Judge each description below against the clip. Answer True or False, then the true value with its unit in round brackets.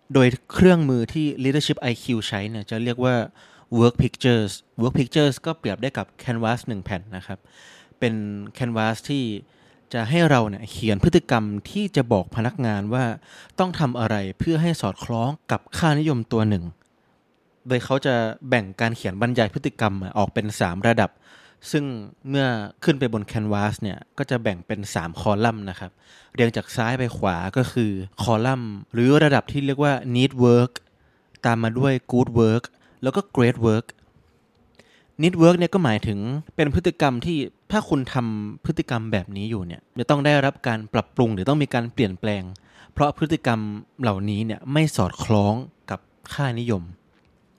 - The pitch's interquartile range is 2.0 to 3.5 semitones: False (4.4 semitones)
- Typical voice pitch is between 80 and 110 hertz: False (120 Hz)